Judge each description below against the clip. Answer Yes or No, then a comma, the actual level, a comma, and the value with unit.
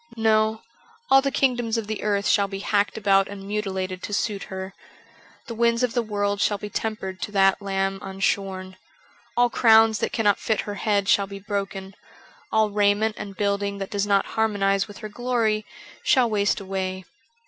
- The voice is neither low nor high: No, high, 205 Hz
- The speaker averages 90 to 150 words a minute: No, average, 180 wpm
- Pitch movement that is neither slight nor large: No, narrow, 1.9 semitones